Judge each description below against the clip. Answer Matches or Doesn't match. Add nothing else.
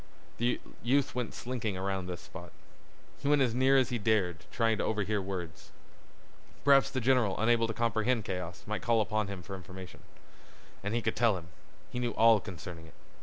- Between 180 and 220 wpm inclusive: Matches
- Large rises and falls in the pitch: Doesn't match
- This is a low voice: Matches